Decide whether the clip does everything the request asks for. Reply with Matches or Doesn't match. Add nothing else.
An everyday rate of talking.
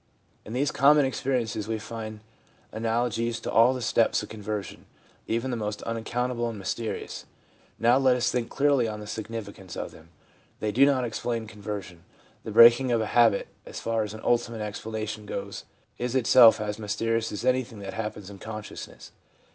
Matches